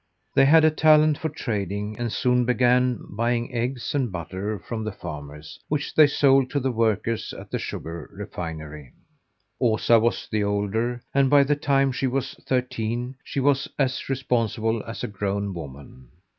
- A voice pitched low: Yes, low, 120 Hz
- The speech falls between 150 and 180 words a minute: Yes, average, 165 wpm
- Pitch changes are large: No, average, 4.8 semitones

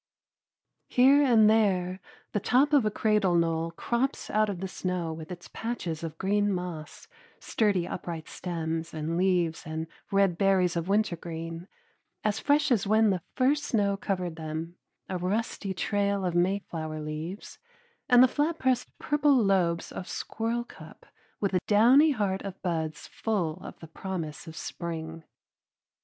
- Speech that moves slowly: No, average, 150 wpm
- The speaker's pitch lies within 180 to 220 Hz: Yes, high, 190 Hz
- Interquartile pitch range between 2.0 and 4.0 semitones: No, average, 4.5 semitones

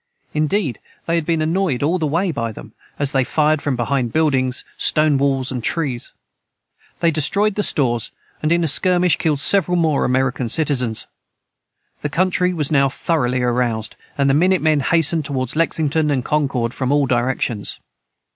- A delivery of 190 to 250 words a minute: No, average, 165 wpm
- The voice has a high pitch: No, medium, 145 Hz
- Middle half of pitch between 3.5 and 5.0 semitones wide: Yes, average, 4.2 semitones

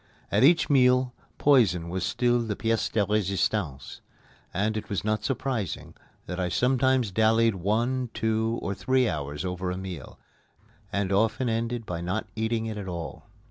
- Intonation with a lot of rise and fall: No, average, 4.3 semitones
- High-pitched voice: No, low, 110 Hz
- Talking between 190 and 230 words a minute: No, average, 160 wpm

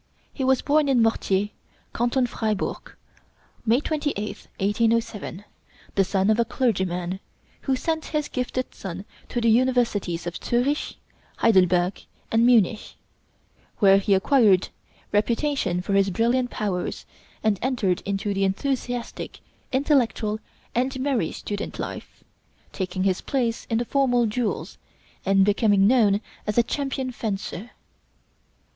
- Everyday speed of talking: No, slow, 125 wpm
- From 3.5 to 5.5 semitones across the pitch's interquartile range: Yes, average, 4.4 semitones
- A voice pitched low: No, high, 225 Hz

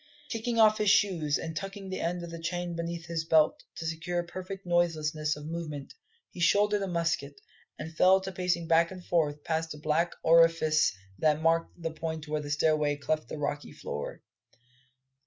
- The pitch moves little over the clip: Yes, narrow, 2.3 semitones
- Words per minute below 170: No, average, 180 wpm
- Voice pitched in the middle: Yes, medium, 165 Hz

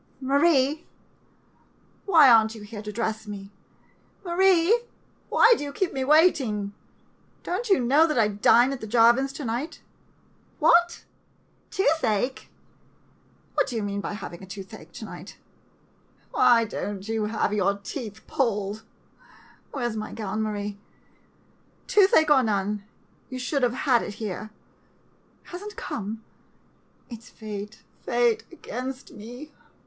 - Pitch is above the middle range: Yes, high, 235 Hz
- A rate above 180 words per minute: No, average, 145 wpm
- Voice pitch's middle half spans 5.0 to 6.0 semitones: Yes, wide, 5.4 semitones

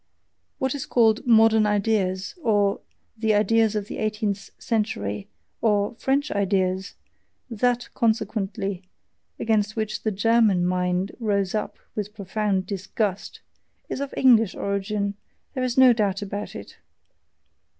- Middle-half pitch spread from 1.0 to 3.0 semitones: Yes, narrow, 2.4 semitones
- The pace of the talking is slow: Yes, slow, 125 wpm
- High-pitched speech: Yes, high, 210 Hz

